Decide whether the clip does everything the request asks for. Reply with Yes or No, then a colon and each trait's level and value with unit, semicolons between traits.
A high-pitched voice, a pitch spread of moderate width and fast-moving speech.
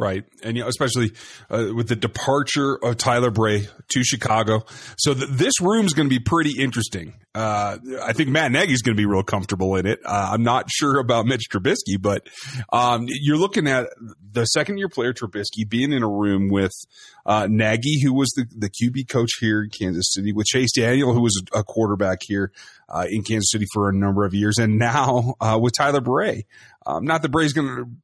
No: low, 115 Hz; average, 4.3 semitones; fast, 215 wpm